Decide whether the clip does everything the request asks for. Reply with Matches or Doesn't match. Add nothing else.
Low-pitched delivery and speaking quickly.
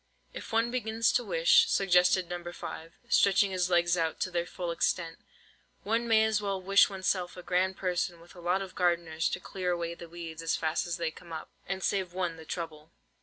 Doesn't match